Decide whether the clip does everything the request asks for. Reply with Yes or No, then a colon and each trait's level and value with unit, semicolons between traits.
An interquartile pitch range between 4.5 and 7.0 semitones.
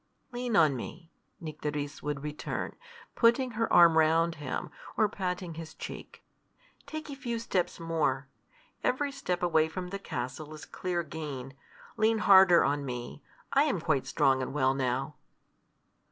Yes: average, 5.3 semitones